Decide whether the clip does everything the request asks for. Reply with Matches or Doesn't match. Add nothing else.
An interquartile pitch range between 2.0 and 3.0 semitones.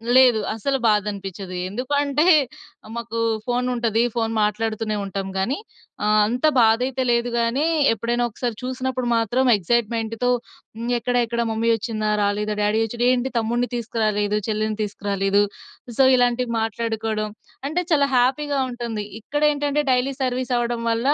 Matches